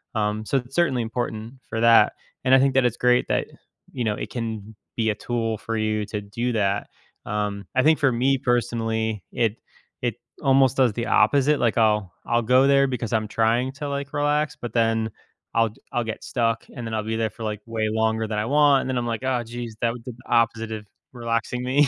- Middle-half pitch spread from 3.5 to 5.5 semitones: No, narrow, 2.5 semitones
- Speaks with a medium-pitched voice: No, low, 115 Hz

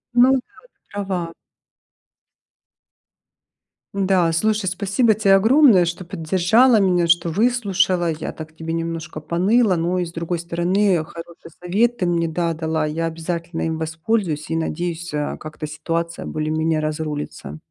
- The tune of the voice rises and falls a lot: No, average, 3.1 semitones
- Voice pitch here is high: No, medium, 170 Hz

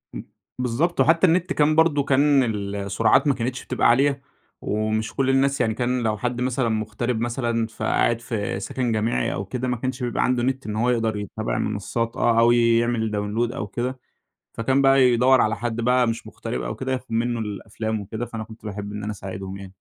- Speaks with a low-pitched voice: Yes, low, 120 Hz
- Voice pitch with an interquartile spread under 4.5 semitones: Yes, average, 2.9 semitones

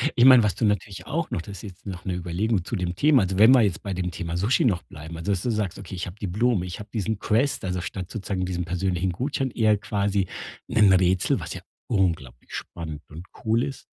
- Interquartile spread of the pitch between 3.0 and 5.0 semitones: Yes, average, 3.5 semitones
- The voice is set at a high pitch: No, very low, 95 Hz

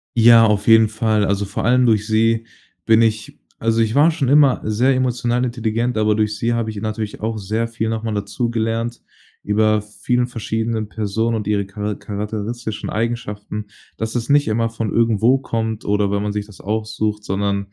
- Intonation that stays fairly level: Yes, narrow, 1.7 semitones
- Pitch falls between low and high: No, low, 110 Hz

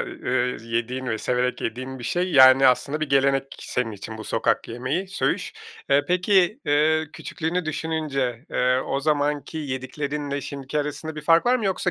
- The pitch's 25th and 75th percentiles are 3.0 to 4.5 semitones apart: Yes, average, 3.7 semitones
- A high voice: No, medium, 140 Hz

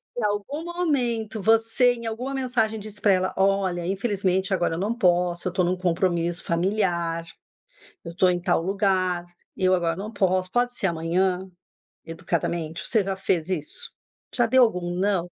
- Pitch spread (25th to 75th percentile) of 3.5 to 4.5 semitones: Yes, average, 3.9 semitones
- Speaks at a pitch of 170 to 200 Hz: Yes, high, 190 Hz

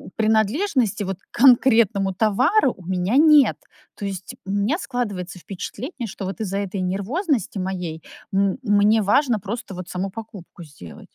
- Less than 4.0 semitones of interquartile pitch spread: No, average, 4.4 semitones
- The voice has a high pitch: Yes, high, 205 Hz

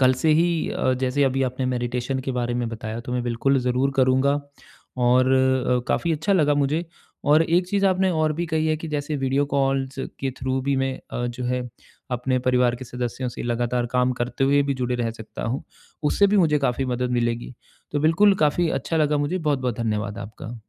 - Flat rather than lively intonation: No, average, 3.1 semitones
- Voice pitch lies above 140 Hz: No, low, 130 Hz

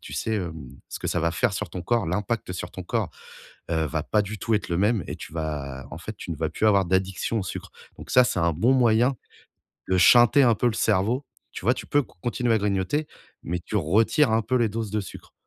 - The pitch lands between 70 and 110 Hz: Yes, low, 105 Hz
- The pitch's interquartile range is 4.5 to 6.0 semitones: Yes, average, 4.9 semitones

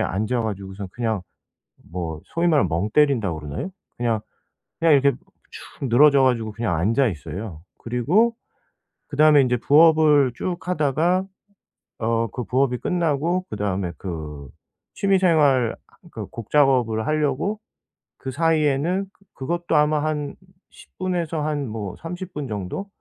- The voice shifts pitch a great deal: Yes, wide, 6.3 semitones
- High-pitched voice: No, low, 135 Hz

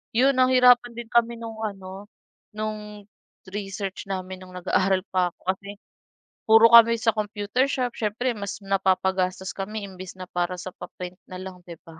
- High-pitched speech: Yes, high, 200 Hz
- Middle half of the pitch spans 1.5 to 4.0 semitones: Yes, average, 3.3 semitones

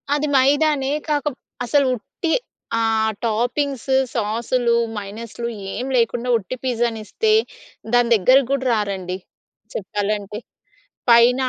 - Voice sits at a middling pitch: No, high, 235 Hz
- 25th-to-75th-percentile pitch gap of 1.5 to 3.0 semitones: No, average, 3.5 semitones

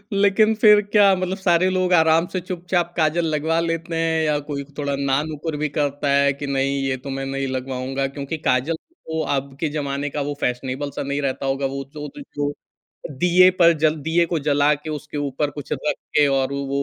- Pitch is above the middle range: No, medium, 150 Hz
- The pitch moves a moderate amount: Yes, average, 3.3 semitones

